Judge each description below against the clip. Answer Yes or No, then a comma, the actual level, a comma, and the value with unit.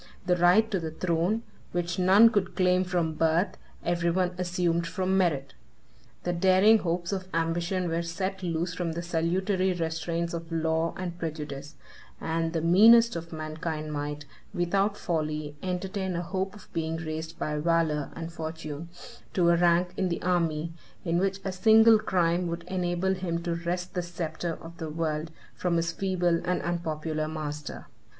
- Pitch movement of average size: No, narrow, 2.0 semitones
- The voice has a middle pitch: Yes, medium, 170 Hz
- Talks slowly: No, average, 165 wpm